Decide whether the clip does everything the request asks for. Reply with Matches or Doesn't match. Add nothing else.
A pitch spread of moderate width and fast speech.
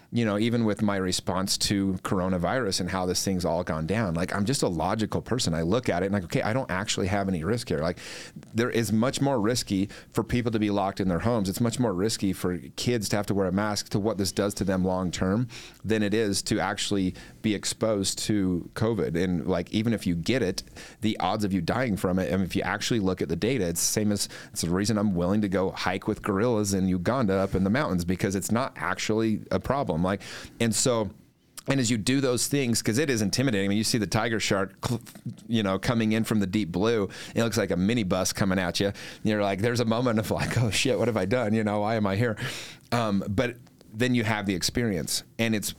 Matches